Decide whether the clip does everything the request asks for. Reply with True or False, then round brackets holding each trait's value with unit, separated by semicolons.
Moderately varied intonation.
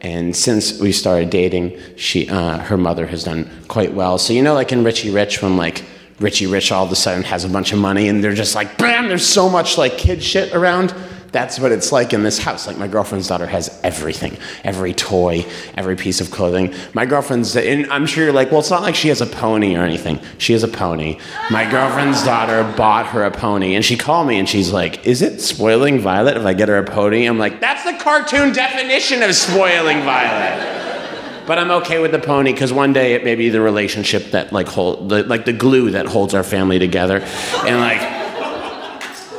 False (6.8 semitones)